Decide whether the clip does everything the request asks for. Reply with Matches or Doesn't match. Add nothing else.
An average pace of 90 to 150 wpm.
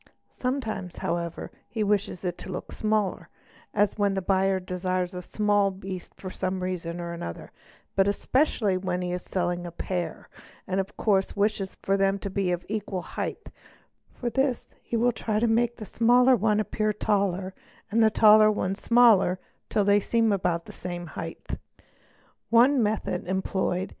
Doesn't match